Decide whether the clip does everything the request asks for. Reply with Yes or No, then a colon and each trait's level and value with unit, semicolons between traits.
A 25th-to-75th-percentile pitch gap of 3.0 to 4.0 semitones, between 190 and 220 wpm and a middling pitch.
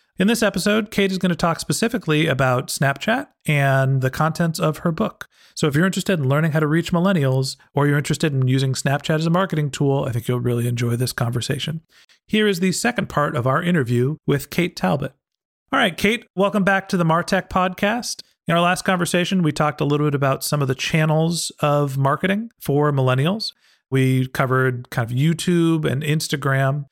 No: average, 5.0 semitones; average, 200 wpm; medium, 155 Hz